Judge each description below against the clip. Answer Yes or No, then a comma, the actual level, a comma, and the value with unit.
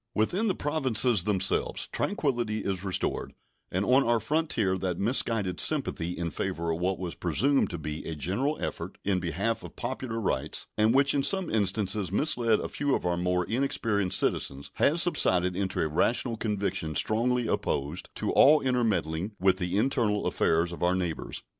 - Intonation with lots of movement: Yes, wide, 5.7 semitones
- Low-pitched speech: Yes, low, 100 Hz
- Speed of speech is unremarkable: Yes, average, 170 wpm